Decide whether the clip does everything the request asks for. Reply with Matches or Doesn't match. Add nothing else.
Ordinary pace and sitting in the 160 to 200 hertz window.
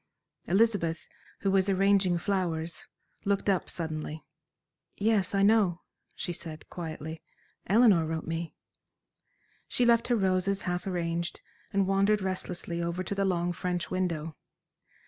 Doesn't match